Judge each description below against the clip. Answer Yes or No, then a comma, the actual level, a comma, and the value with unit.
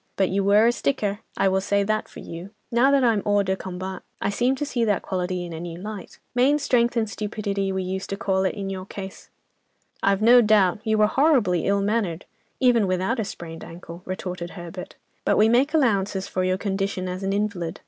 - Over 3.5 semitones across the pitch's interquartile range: No, average, 2.9 semitones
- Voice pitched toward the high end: Yes, high, 200 Hz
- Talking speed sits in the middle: No, fast, 215 wpm